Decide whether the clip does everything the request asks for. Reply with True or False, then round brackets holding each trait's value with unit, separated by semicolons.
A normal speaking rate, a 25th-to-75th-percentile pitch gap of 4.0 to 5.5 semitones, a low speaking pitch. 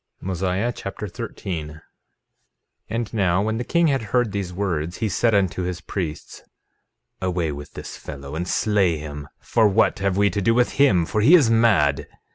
True (180 wpm; 4.6 semitones; 95 Hz)